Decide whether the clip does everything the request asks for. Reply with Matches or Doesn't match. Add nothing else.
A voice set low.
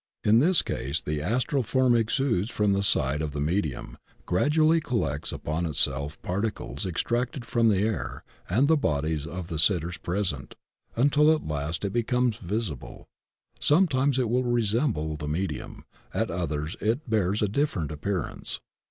Matches